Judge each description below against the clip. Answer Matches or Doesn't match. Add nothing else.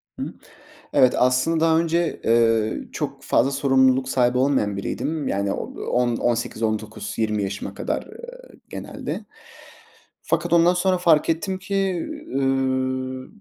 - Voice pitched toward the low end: Matches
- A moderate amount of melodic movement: Doesn't match